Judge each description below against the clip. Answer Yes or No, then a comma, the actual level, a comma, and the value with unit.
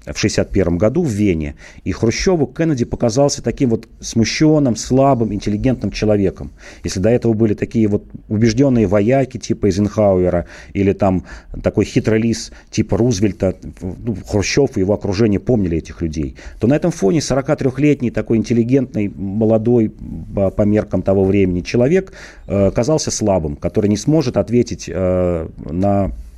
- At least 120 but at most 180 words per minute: Yes, average, 140 wpm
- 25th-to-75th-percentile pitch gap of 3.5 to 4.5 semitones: Yes, average, 4.1 semitones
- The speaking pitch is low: Yes, low, 105 Hz